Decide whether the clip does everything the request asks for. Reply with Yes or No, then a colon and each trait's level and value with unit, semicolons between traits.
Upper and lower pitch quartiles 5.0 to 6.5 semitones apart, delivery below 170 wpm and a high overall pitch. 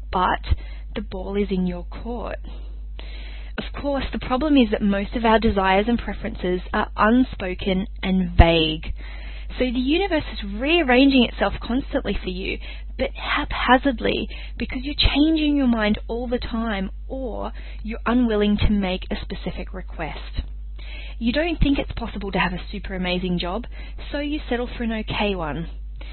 Yes: wide, 5.4 semitones; average, 155 wpm; high, 210 Hz